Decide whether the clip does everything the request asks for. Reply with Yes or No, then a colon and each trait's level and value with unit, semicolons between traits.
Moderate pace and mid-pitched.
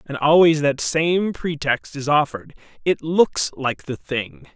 Yes: average, 145 wpm; medium, 145 Hz